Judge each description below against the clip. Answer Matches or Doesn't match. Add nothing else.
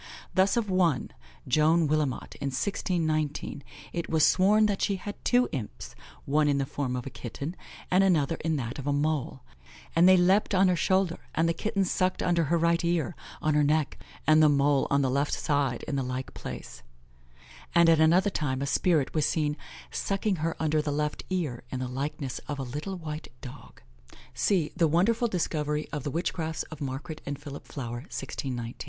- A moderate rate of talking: Matches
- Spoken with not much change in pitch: Doesn't match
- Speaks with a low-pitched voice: Doesn't match